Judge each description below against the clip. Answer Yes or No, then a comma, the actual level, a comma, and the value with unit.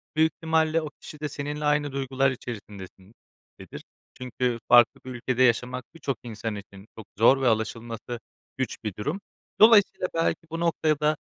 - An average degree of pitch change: Yes, average, 4.8 semitones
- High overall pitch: No, low, 130 Hz